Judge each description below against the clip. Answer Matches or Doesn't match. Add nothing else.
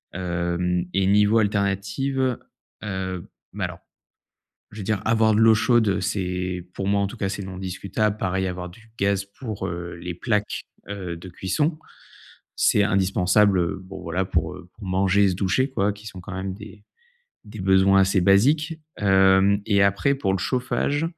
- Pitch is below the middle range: Matches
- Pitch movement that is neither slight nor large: Doesn't match